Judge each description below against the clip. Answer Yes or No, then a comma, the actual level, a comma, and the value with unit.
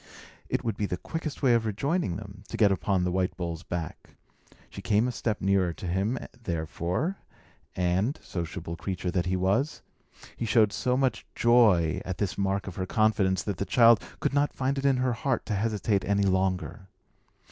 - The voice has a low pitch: Yes, low, 100 Hz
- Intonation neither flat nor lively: Yes, average, 4.3 semitones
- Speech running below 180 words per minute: No, average, 190 wpm